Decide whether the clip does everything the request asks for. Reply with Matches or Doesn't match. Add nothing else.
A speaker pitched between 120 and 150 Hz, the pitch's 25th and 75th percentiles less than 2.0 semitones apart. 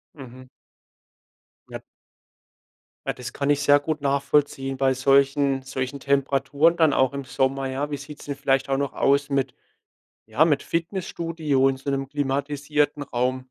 Matches